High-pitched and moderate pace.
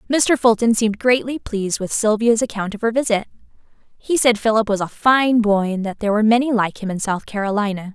No: high, 220 Hz; fast, 210 wpm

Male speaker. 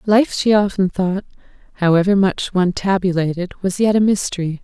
No: female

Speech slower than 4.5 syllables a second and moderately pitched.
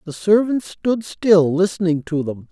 Yes: 4.2 syllables/s; medium, 180 Hz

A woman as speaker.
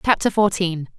Yes: female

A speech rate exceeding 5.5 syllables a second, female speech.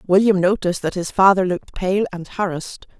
Yes: 6.0 syllables/s; female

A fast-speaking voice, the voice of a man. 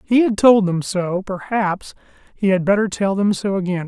No: average, 185 wpm; male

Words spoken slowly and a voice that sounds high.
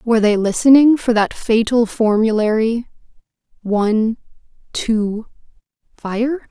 Yes: slow, 65 wpm; high, 225 Hz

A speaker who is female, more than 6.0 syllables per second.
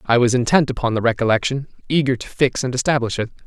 No: male; 6.6 syllables/s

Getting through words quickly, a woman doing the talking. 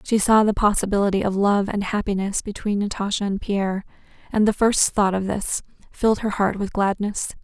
No: average, 185 wpm; female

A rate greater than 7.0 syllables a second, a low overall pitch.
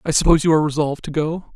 No: 8.3 syllables/s; medium, 155 Hz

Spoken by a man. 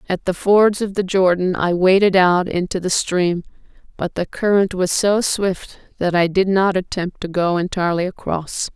No: female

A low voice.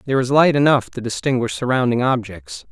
Yes: low, 125 Hz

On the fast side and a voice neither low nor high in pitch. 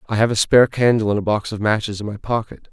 No: fast, 285 wpm; low, 110 Hz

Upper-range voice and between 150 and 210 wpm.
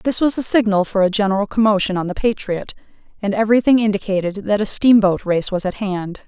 Yes: high, 205 Hz; average, 200 wpm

